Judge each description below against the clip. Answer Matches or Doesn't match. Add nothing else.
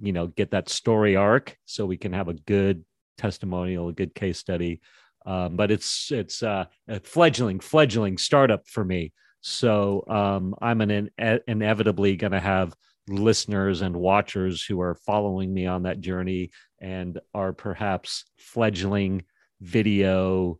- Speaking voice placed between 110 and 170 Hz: Doesn't match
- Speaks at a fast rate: Doesn't match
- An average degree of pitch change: Doesn't match